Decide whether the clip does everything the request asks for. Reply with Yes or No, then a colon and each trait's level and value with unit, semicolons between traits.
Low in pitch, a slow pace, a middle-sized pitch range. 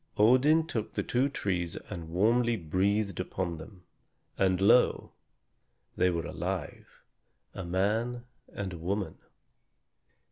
Yes: low, 100 Hz; slow, 115 wpm; average, 4.5 semitones